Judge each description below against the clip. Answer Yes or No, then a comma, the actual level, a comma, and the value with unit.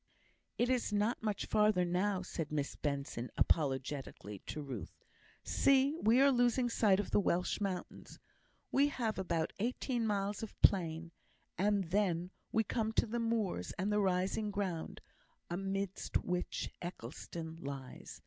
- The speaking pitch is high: Yes, high, 195 Hz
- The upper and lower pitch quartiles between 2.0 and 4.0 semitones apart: No, average, 4.8 semitones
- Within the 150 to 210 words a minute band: No, average, 140 wpm